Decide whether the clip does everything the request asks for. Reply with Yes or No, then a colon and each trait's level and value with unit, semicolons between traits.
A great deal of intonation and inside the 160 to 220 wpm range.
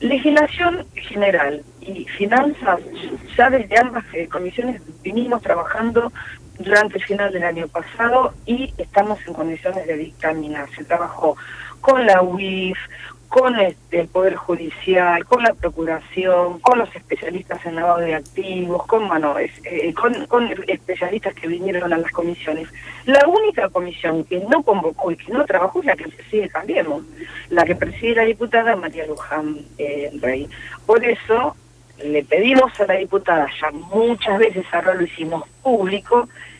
No: wide, 6.0 semitones; average, 150 wpm